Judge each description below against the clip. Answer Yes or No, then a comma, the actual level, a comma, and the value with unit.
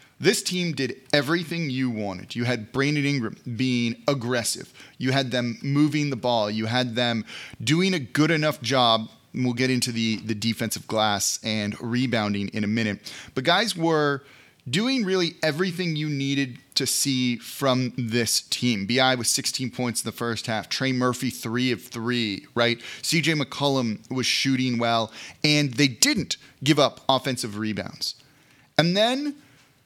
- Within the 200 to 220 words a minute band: No, average, 160 wpm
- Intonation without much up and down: No, average, 3.6 semitones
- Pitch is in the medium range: No, low, 125 Hz